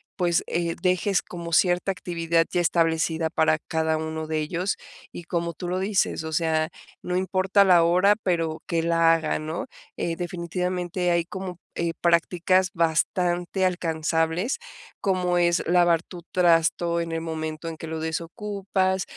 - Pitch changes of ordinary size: No, narrow, 1.8 semitones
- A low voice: No, medium, 170 Hz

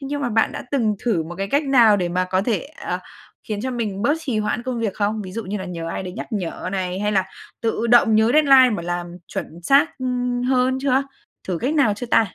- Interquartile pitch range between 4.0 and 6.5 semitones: Yes, average, 5.0 semitones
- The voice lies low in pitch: No, high, 220 Hz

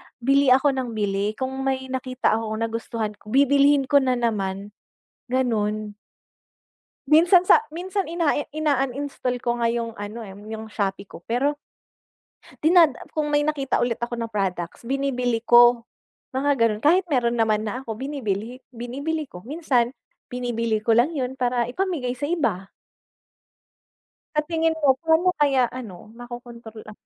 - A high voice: Yes, high, 245 Hz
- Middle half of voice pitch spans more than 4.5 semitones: No, average, 4.2 semitones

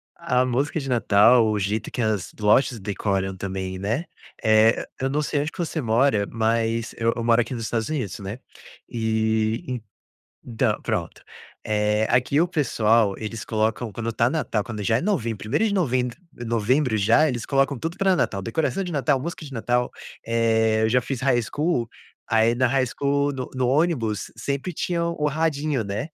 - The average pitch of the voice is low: Yes, low, 120 Hz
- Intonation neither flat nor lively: Yes, average, 4.2 semitones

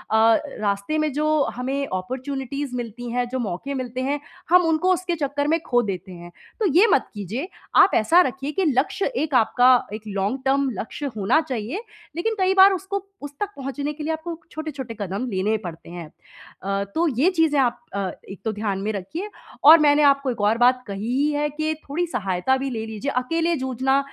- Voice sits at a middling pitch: No, very high, 265 Hz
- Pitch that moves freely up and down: Yes, wide, 5.9 semitones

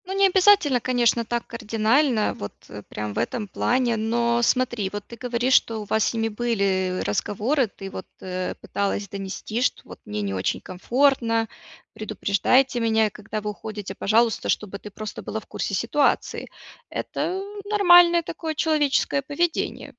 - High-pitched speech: Yes, high, 230 Hz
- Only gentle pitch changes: No, average, 4.3 semitones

